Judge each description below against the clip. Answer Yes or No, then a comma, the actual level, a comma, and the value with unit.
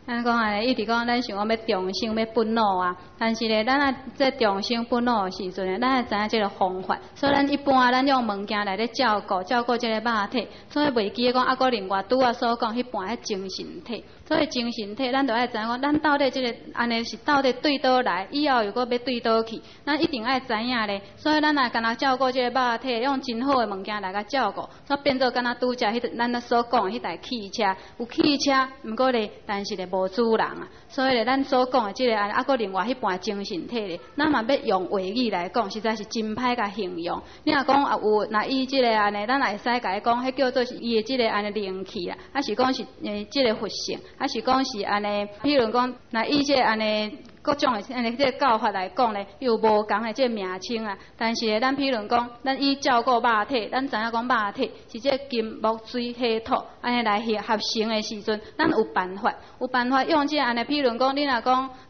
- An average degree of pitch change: Yes, average, 3.5 semitones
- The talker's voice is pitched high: Yes, high, 240 Hz